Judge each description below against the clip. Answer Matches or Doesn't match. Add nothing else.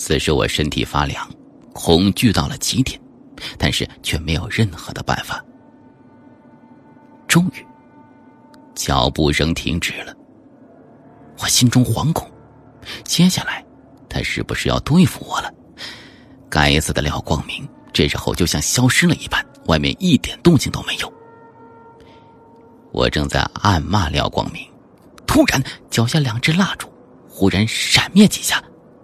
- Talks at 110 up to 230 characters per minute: Matches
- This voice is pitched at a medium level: Doesn't match